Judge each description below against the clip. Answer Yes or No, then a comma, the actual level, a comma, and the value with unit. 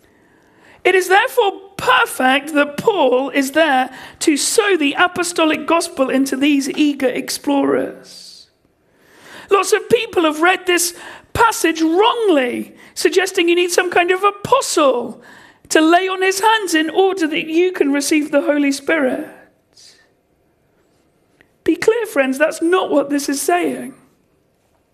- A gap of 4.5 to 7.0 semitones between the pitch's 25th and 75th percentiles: Yes, average, 4.8 semitones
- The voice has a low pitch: No, very high, 340 Hz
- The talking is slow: Yes, slow, 130 wpm